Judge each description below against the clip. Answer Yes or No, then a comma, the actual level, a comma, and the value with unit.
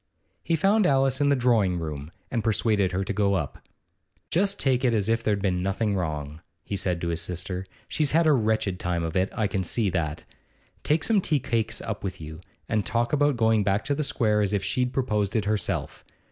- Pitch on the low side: Yes, low, 105 Hz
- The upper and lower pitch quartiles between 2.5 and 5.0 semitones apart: No, wide, 5.5 semitones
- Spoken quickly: Yes, fast, 220 wpm